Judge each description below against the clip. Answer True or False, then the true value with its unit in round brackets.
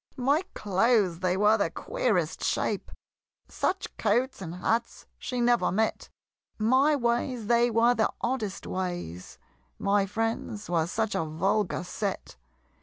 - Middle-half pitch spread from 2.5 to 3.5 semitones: False (4.2 semitones)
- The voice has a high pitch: True (220 Hz)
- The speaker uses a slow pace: True (130 wpm)